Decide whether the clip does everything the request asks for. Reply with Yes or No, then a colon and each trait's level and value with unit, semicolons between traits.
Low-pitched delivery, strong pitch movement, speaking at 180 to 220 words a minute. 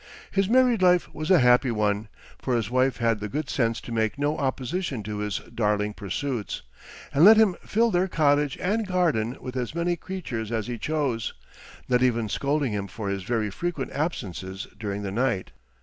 Yes: low, 125 Hz; wide, 6.8 semitones; average, 185 wpm